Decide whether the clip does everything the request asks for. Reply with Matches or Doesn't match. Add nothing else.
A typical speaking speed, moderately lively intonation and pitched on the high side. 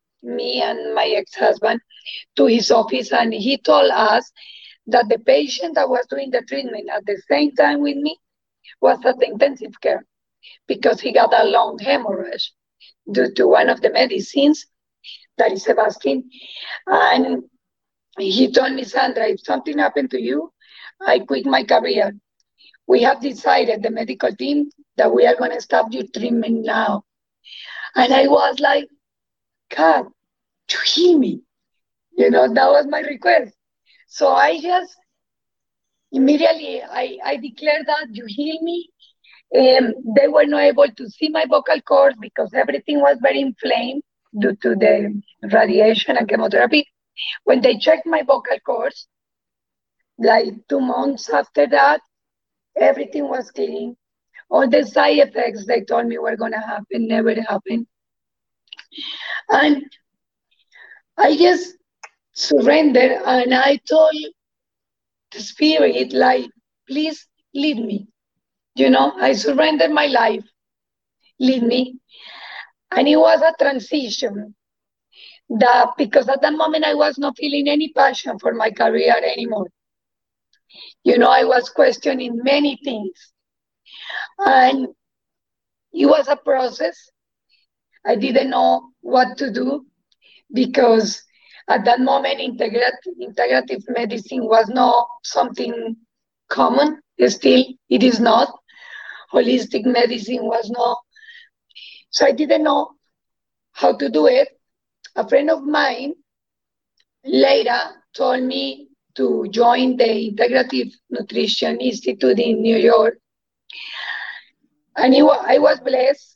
Doesn't match